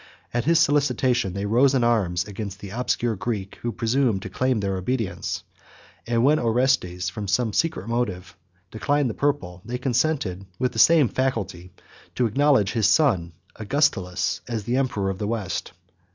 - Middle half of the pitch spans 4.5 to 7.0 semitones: Yes, average, 5.0 semitones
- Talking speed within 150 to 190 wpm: Yes, average, 165 wpm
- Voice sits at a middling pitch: No, low, 115 Hz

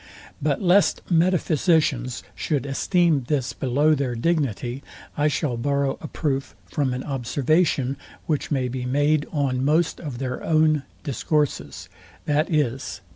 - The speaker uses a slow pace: Yes, slow, 130 wpm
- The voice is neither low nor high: Yes, medium, 145 Hz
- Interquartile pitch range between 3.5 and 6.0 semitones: No, average, 3.1 semitones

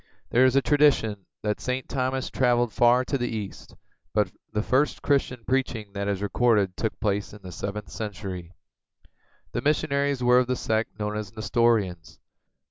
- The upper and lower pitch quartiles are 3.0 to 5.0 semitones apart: Yes, average, 3.9 semitones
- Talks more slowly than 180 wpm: Yes, average, 165 wpm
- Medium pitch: No, low, 115 Hz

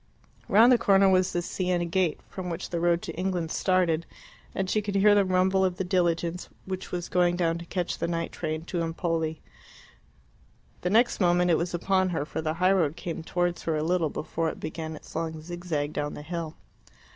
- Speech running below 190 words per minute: No, fast, 205 wpm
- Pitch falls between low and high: Yes, medium, 175 Hz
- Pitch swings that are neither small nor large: No, narrow, 2.1 semitones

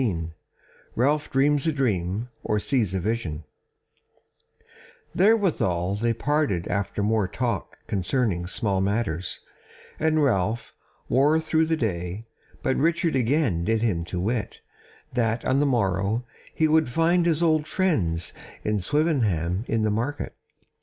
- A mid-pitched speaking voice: No, low, 115 Hz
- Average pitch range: No, wide, 7.5 semitones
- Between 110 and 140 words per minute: Yes, slow, 135 wpm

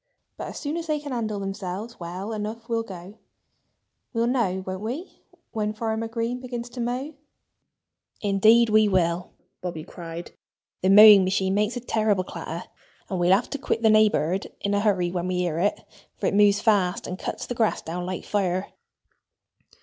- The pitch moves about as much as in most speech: Yes, average, 3.8 semitones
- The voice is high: Yes, high, 205 Hz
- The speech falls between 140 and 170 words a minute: No, average, 180 wpm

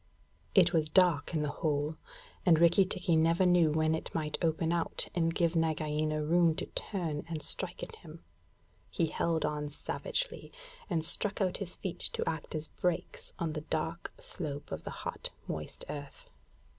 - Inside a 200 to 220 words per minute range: No, average, 170 wpm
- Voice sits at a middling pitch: Yes, medium, 165 Hz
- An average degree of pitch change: No, narrow, 2.3 semitones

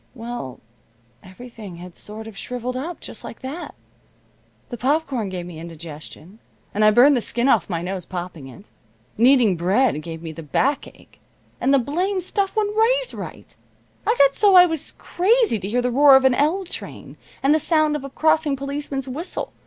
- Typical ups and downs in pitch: No, wide, 8.1 semitones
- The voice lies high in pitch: Yes, very high, 255 Hz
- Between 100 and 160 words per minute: No, average, 185 wpm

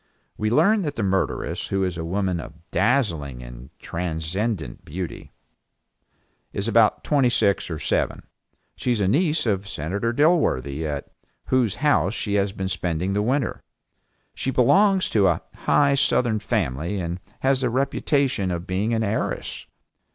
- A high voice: No, low, 100 Hz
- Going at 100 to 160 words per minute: Yes, average, 150 wpm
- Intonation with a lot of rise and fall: Yes, wide, 6.6 semitones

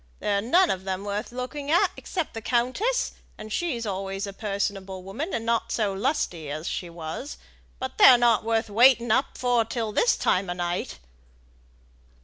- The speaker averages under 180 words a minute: Yes, average, 170 wpm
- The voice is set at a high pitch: Yes, high, 220 Hz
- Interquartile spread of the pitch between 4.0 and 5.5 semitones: Yes, average, 4.5 semitones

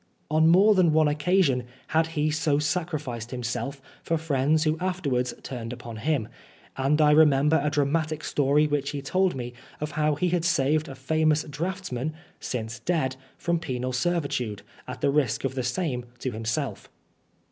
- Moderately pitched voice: Yes, medium, 150 Hz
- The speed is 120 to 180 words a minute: Yes, average, 165 wpm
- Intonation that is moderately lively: Yes, average, 3.7 semitones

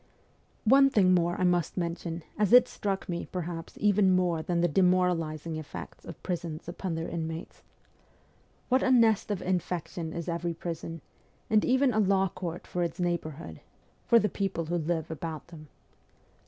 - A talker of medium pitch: Yes, medium, 175 Hz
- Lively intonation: No, average, 2.7 semitones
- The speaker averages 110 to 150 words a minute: No, average, 170 wpm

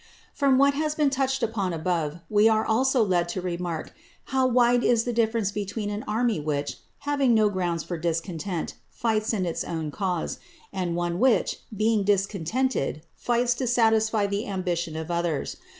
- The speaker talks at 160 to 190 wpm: Yes, average, 170 wpm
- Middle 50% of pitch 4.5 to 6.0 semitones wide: Yes, wide, 5.4 semitones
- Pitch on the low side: No, high, 205 Hz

